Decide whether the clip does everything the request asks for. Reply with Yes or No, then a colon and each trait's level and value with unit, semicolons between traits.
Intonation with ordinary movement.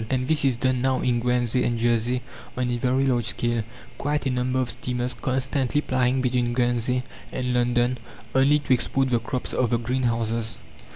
No: narrow, 1.4 semitones